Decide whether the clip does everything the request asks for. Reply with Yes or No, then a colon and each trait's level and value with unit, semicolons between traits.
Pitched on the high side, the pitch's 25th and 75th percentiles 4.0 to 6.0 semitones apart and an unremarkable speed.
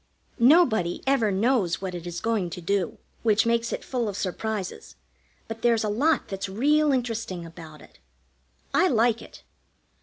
Yes: high, 220 Hz; average, 4.4 semitones; average, 160 wpm